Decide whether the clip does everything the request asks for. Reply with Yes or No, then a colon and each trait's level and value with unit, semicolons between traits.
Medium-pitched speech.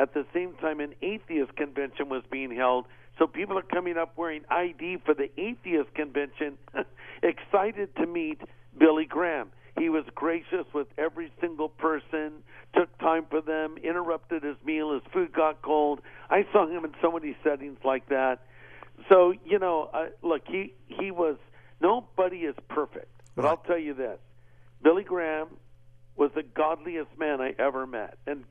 Yes: medium, 155 Hz